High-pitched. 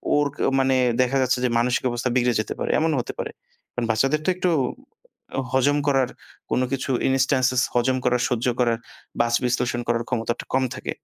No: low, 125 Hz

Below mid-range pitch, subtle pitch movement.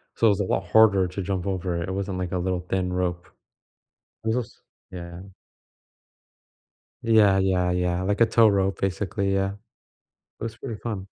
Yes: very low, 95 Hz; narrow, 2.2 semitones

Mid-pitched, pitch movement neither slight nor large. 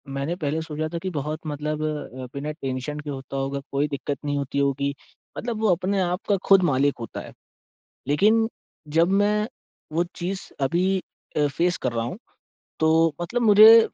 Yes: medium, 155 Hz; average, 4.7 semitones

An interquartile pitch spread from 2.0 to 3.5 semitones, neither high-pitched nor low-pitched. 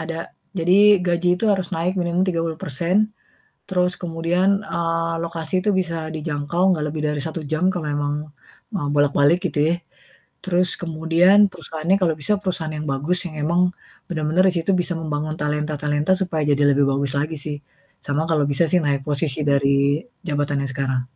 Yes: average, 3.0 semitones; medium, 160 Hz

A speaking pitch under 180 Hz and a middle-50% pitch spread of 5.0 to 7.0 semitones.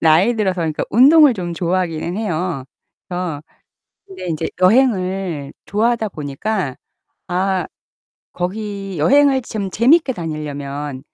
No: medium, 185 Hz; wide, 5.5 semitones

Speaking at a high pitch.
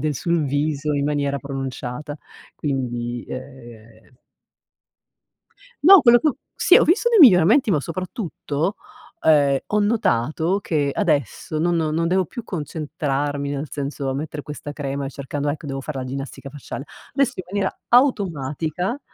No: medium, 150 Hz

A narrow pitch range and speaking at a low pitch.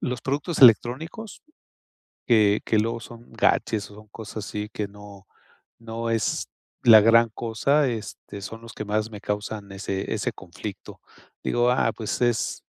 Yes: narrow, 2.3 semitones; low, 110 Hz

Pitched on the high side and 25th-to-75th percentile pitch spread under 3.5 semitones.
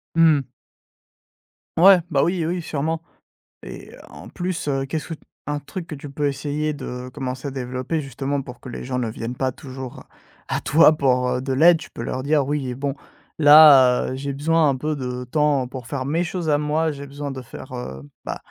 No: medium, 140 Hz; average, 3.0 semitones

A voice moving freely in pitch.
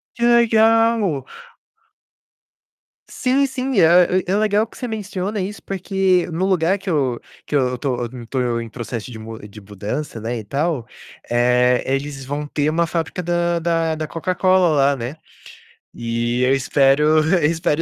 Yes: wide, 6.9 semitones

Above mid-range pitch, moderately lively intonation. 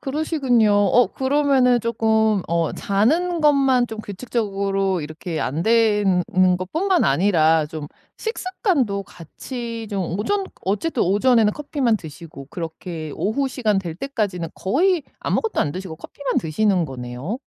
No: high, 210 Hz; wide, 6.7 semitones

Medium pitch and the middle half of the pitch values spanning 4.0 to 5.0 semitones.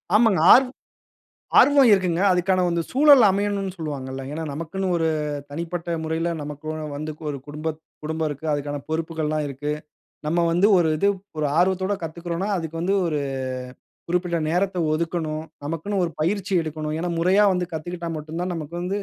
No: medium, 170 Hz; average, 3.2 semitones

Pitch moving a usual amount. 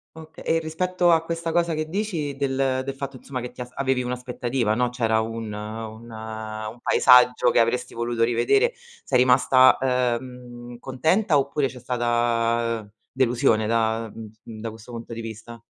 Yes: average, 3.0 semitones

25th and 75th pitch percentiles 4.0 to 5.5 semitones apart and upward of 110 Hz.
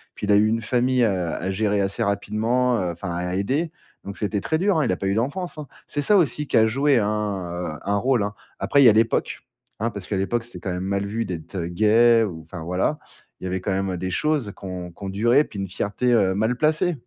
No: average, 4.5 semitones; low, 105 Hz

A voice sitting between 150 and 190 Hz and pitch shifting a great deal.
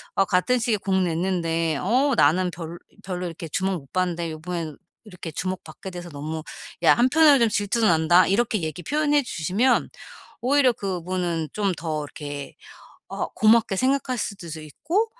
Yes: medium, 185 Hz; wide, 6.0 semitones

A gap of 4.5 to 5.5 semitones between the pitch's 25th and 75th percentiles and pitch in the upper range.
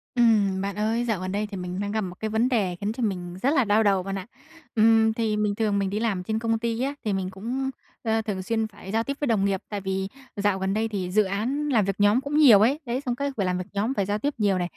No: average, 2.9 semitones; high, 210 Hz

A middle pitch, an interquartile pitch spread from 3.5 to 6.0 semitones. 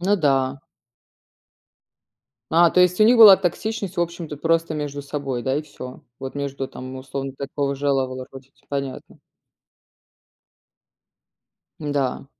Yes: medium, 145 Hz; average, 3.9 semitones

